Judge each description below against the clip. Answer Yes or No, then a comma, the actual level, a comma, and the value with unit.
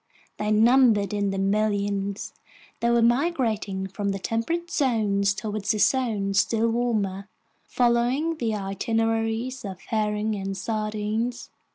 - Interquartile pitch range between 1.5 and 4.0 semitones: Yes, average, 2.9 semitones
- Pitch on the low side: No, high, 215 Hz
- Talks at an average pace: No, slow, 120 wpm